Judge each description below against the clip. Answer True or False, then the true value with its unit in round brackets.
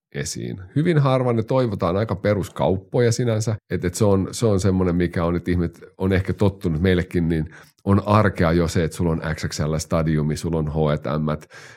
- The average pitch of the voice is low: True (90 Hz)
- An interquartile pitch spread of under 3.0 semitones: False (3.9 semitones)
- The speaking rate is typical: False (175 wpm)